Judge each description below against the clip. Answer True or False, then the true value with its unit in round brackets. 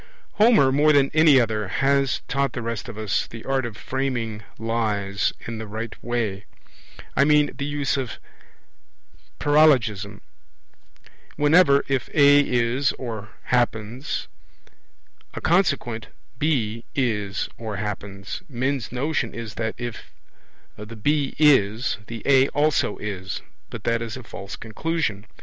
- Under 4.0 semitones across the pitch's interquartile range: False (4.3 semitones)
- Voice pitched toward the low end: True (120 Hz)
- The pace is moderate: False (130 wpm)